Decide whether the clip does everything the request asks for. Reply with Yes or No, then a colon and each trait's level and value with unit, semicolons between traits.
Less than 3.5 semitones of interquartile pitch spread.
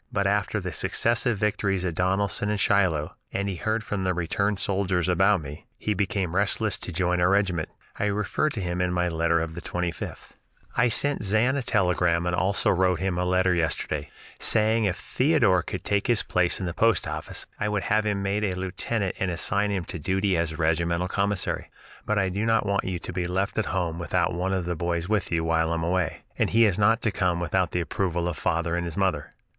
Yes: average, 2.8 semitones